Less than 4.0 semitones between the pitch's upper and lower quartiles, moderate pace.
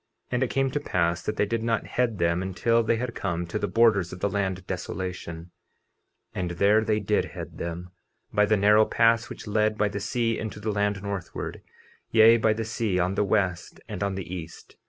No: average, 3.4 semitones; fast, 215 wpm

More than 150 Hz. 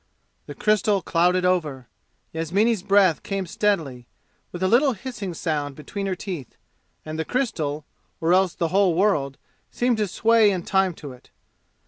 Yes: medium, 185 Hz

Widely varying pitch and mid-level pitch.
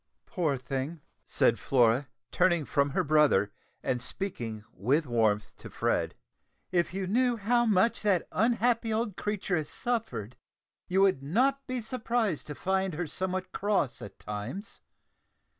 Yes: wide, 8.0 semitones; medium, 180 Hz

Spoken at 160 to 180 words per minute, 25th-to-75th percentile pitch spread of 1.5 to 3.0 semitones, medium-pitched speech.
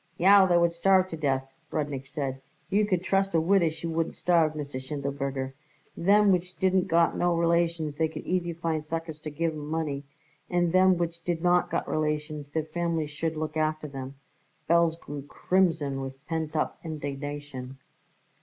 Yes: average, 170 wpm; average, 2.7 semitones; medium, 160 Hz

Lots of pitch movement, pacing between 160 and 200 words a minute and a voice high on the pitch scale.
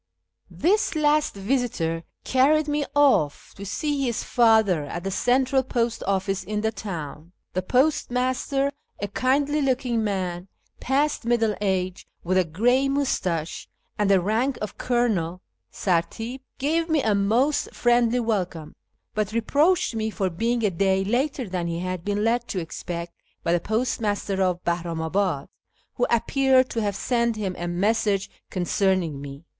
No: wide, 5.7 semitones; average, 150 wpm; high, 215 Hz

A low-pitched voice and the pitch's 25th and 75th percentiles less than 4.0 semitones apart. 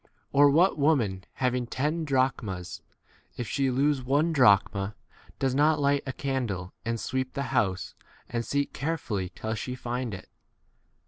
No: low, 130 Hz; average, 4.3 semitones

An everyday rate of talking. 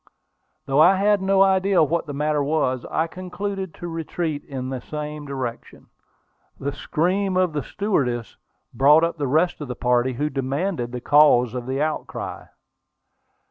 Yes: average, 160 wpm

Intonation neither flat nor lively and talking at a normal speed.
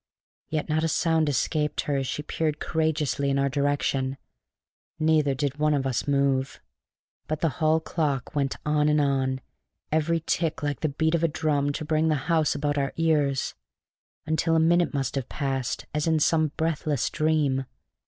No: narrow, 2.3 semitones; average, 175 wpm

